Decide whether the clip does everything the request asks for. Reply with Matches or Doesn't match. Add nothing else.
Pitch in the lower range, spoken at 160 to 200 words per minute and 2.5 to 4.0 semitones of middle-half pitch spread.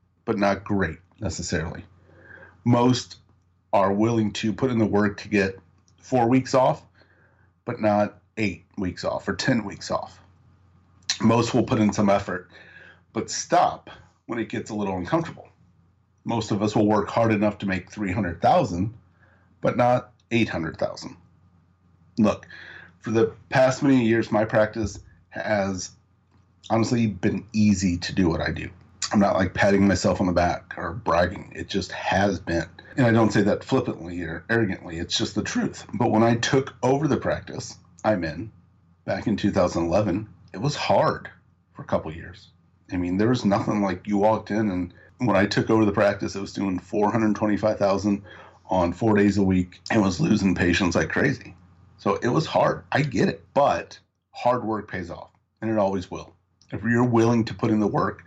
Matches